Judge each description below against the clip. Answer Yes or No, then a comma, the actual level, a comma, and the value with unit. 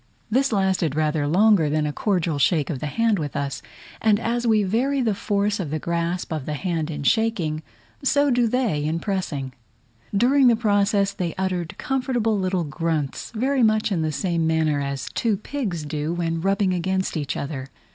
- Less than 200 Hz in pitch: Yes, medium, 185 Hz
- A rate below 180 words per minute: No, average, 185 wpm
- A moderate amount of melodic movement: No, wide, 5.8 semitones